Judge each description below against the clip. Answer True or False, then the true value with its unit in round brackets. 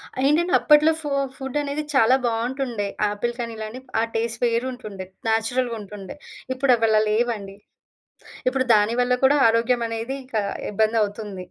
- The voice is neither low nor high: False (230 Hz)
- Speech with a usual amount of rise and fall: True (3.0 semitones)